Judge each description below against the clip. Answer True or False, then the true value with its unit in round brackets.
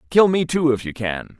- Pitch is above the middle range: False (135 Hz)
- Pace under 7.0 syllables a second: True (5.5 syllables/s)